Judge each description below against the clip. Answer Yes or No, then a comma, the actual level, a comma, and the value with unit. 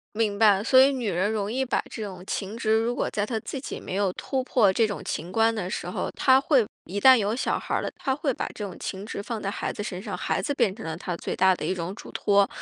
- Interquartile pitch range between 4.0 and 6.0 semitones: No, average, 3.5 semitones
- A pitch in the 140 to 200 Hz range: No, high, 210 Hz